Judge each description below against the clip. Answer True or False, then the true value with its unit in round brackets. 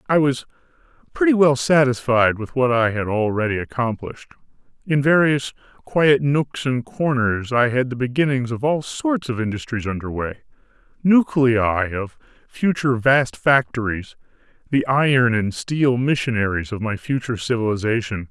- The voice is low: True (125 Hz)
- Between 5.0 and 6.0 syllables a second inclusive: False (4.8 syllables/s)